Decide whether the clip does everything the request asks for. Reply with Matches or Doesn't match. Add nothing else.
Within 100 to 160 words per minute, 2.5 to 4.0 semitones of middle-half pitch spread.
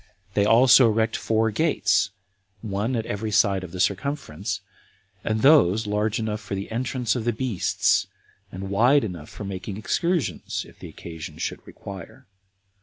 Matches